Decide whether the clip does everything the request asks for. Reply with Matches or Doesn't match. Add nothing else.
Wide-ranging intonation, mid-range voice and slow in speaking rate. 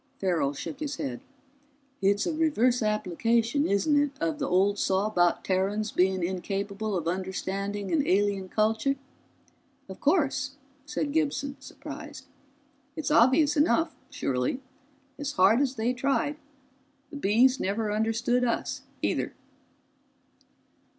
Doesn't match